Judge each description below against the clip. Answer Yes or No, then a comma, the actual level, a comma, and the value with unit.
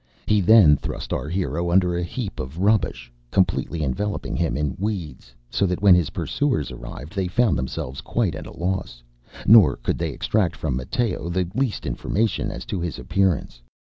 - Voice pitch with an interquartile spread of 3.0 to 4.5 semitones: No, average, 5.2 semitones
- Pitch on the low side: Yes, very low, 90 Hz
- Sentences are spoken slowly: No, average, 175 wpm